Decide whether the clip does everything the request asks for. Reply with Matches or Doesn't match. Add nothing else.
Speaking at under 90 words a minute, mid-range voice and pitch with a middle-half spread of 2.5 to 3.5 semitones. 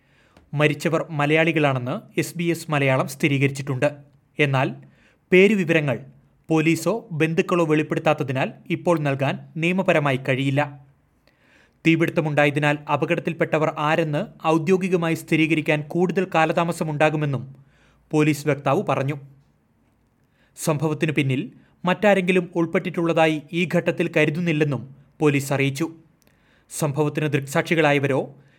Matches